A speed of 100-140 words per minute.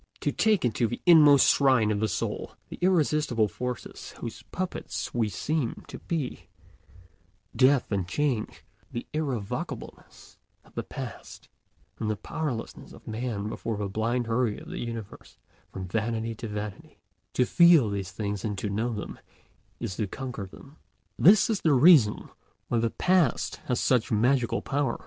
No: average, 150 wpm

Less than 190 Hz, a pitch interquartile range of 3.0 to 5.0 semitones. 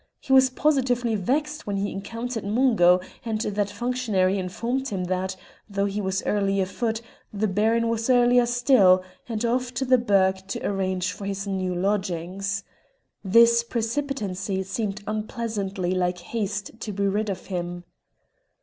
No: high, 205 Hz; average, 3.6 semitones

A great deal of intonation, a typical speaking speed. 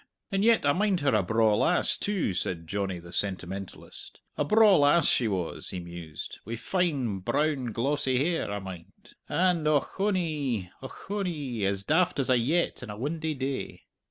Yes: wide, 8.9 semitones; average, 165 wpm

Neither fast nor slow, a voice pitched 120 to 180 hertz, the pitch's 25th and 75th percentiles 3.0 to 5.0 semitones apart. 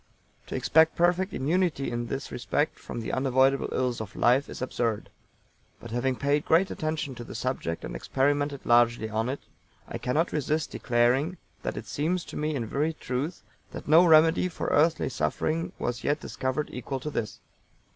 Yes: average, 175 wpm; medium, 140 Hz; average, 4.3 semitones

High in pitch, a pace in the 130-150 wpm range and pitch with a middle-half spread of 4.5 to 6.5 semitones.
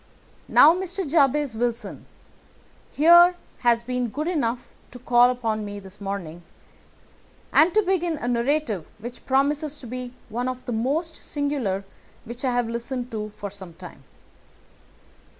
Yes: high, 245 Hz; average, 145 wpm; average, 4.9 semitones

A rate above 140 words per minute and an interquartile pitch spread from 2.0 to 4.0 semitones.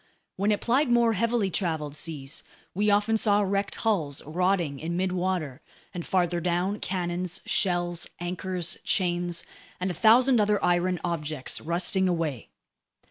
No: slow, 135 wpm; average, 3.0 semitones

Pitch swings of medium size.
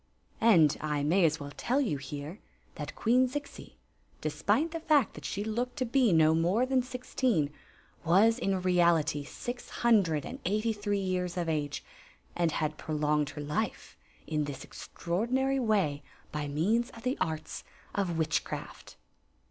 No: wide, 7.5 semitones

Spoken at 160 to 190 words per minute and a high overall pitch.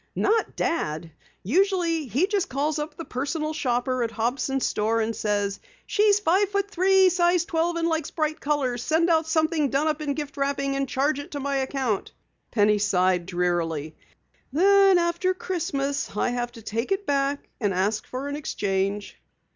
Yes: average, 170 wpm; very high, 280 Hz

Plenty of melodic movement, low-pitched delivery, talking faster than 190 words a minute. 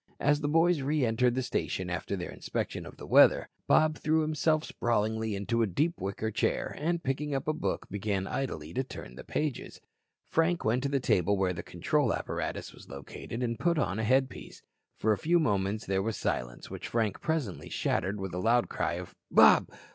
Yes: wide, 7.1 semitones; low, 115 Hz; average, 200 wpm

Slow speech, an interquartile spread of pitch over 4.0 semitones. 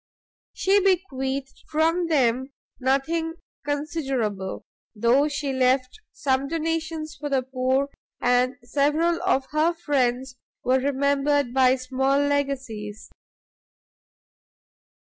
No: slow, 95 wpm; average, 3.0 semitones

